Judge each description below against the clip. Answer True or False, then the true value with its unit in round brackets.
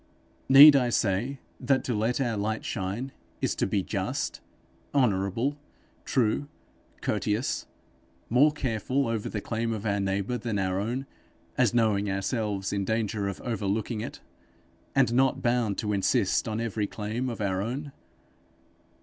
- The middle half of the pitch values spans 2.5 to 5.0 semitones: True (3.5 semitones)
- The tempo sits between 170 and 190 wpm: False (145 wpm)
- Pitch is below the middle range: True (110 Hz)